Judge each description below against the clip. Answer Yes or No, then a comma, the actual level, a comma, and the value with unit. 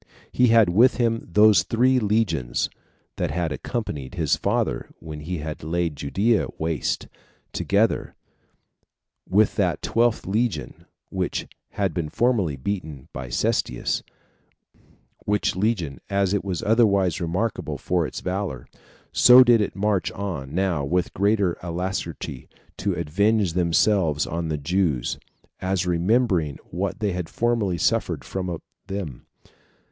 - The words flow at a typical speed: No, slow, 125 wpm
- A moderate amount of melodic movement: Yes, average, 4.4 semitones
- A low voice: Yes, very low, 95 Hz